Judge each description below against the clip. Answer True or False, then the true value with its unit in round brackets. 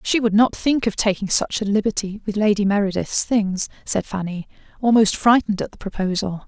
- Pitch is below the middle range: False (205 Hz)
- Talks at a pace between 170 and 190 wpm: True (185 wpm)